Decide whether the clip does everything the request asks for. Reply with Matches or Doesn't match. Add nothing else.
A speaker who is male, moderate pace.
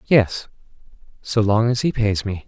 Matches